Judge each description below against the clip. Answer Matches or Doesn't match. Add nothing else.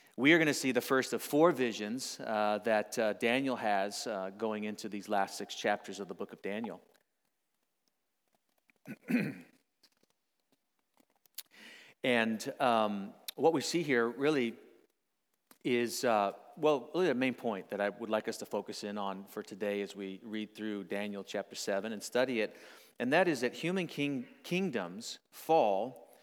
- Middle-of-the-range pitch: Doesn't match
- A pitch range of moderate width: Matches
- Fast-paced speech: Doesn't match